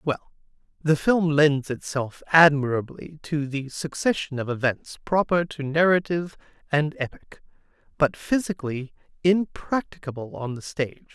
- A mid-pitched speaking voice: Yes, medium, 150 Hz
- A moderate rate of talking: No, slow, 120 wpm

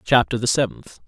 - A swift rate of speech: No, average, 170 wpm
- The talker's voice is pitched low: Yes, low, 115 Hz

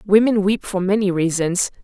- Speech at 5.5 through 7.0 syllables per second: No, 5.0 syllables/s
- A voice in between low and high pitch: No, high, 195 Hz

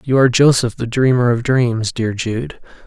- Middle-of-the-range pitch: No, low, 120 Hz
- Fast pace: No, average, 190 wpm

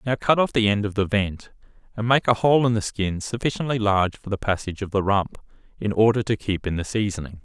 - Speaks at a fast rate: Yes, fast, 240 wpm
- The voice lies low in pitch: Yes, low, 105 Hz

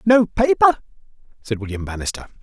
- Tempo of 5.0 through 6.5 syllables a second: Yes, 5.5 syllables/s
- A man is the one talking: Yes, male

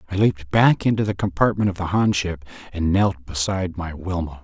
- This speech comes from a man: Yes, male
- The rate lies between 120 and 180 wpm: No, fast, 205 wpm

